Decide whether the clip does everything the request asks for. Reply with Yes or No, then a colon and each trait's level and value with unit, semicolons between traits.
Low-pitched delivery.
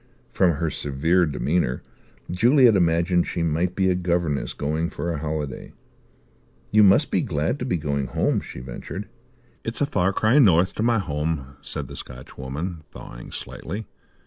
Yes: very low, 85 Hz